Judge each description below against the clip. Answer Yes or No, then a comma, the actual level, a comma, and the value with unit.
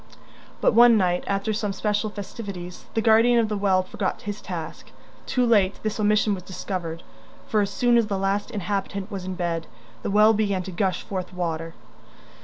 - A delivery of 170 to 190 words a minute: Yes, average, 185 wpm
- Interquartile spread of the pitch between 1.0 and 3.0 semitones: Yes, average, 2.7 semitones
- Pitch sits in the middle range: No, high, 200 Hz